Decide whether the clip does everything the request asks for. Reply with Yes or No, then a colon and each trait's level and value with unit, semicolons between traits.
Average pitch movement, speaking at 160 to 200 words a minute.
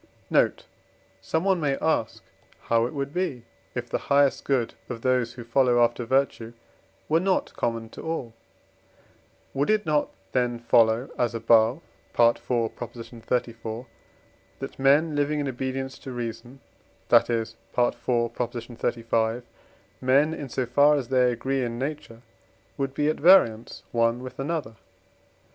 No: average, 3.2 semitones; average, 140 wpm